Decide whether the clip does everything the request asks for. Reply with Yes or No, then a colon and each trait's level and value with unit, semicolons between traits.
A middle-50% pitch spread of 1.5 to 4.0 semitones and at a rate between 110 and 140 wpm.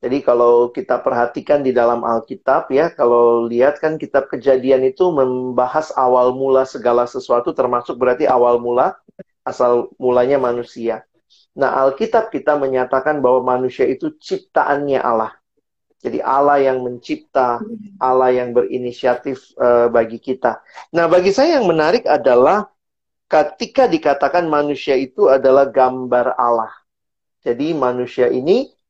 Yes: average, 2.8 semitones; average, 125 wpm